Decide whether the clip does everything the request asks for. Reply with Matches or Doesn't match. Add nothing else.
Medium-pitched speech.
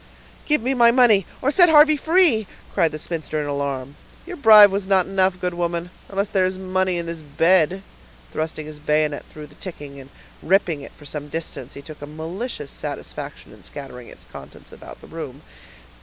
Matches